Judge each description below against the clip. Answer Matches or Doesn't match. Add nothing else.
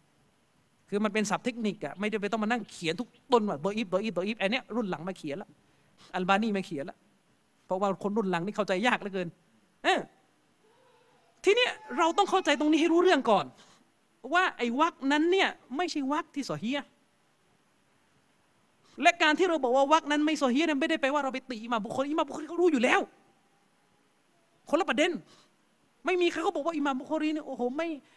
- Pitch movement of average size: Doesn't match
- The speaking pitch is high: Matches